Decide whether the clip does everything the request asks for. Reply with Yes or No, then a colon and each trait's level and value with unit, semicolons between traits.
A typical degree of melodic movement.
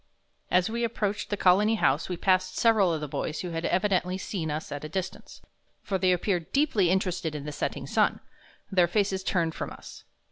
Yes: average, 3.3 semitones